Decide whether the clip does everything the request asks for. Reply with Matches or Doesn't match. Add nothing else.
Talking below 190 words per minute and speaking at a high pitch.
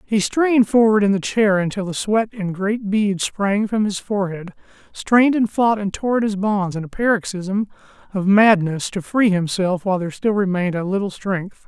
Doesn't match